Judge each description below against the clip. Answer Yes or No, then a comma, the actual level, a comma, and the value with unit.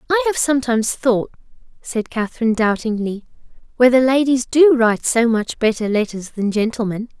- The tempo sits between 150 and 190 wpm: No, average, 140 wpm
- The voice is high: Yes, high, 240 Hz